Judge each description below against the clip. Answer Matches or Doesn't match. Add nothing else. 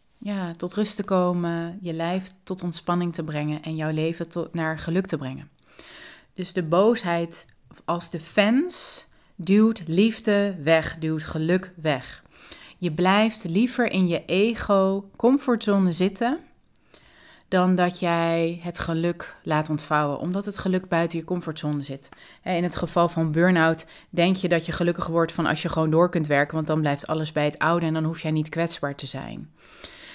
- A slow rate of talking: Doesn't match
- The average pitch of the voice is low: Doesn't match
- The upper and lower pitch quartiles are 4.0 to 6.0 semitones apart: Doesn't match